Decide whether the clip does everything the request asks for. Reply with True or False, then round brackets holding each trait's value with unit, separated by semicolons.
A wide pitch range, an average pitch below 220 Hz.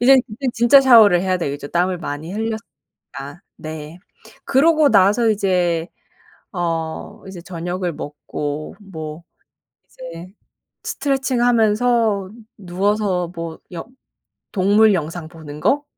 False (5.0 semitones; 185 Hz)